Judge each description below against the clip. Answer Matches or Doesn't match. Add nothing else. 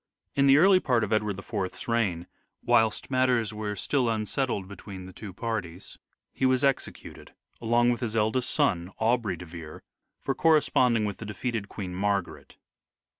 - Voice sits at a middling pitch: Doesn't match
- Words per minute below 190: Matches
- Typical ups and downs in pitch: Matches